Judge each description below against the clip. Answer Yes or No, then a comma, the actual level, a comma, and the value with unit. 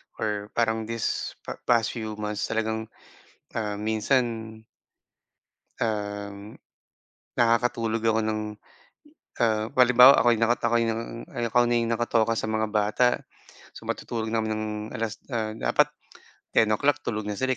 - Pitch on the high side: No, low, 110 Hz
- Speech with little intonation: Yes, narrow, 1.4 semitones